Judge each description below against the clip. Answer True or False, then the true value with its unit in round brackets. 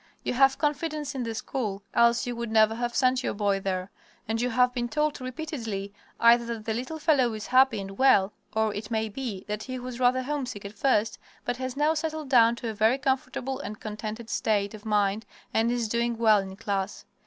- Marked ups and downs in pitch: False (3.4 semitones)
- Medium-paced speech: False (210 wpm)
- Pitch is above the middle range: True (235 Hz)